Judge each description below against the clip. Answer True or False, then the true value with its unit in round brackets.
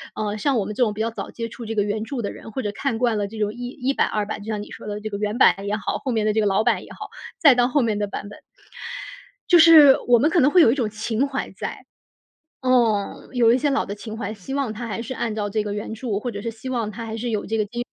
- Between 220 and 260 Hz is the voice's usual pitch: True (225 Hz)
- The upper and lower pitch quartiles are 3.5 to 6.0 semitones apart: False (2.9 semitones)